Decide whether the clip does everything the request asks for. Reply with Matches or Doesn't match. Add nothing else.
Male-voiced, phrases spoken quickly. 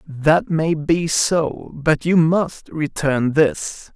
Doesn't match